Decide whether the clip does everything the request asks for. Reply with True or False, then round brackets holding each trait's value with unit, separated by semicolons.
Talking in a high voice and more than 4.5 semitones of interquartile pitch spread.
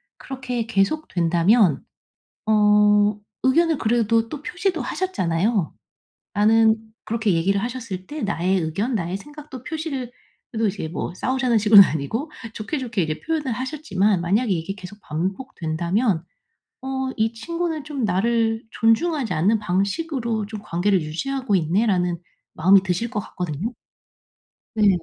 True (215 Hz; 5.4 semitones)